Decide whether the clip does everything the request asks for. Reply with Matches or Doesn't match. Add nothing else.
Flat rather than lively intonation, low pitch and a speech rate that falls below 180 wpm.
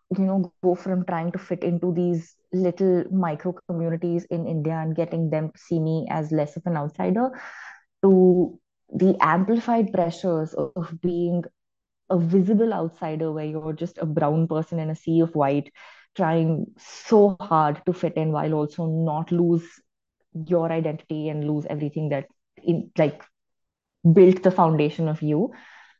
Doesn't match